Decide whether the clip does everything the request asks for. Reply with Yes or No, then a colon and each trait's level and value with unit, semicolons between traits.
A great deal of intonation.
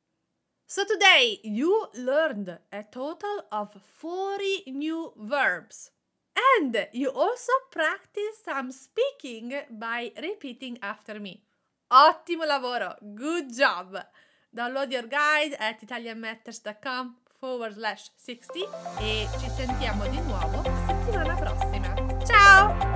Yes: wide, 7.4 semitones